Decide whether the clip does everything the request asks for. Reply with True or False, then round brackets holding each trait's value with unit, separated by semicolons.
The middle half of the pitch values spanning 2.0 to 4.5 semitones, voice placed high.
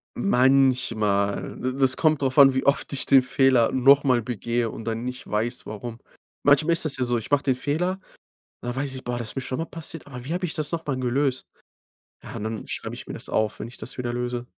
False (2.7 semitones; 130 Hz)